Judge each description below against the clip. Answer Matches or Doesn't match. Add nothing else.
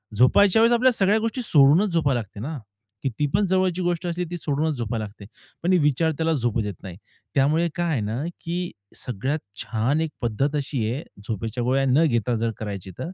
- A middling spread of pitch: Doesn't match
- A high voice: Doesn't match